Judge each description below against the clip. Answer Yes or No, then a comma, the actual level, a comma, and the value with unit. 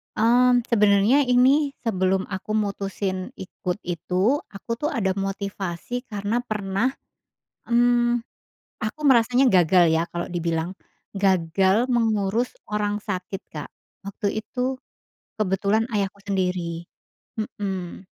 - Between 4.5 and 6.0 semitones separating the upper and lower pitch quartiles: No, average, 4.0 semitones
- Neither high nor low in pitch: No, high, 200 Hz